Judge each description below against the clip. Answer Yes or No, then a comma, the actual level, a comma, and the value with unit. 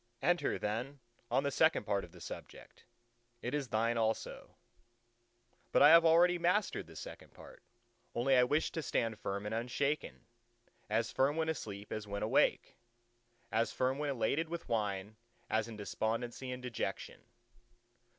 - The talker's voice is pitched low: Yes, low, 120 Hz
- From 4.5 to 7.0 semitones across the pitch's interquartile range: Yes, average, 4.9 semitones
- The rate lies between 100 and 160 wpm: Yes, average, 150 wpm